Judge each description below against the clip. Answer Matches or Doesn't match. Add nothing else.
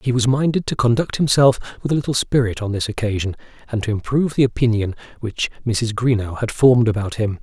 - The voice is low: Matches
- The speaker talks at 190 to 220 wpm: Matches